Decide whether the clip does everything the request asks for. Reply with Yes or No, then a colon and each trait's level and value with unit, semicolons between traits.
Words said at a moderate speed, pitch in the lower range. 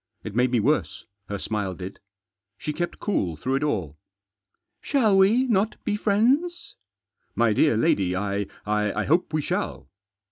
Yes: average, 175 wpm; low, 120 Hz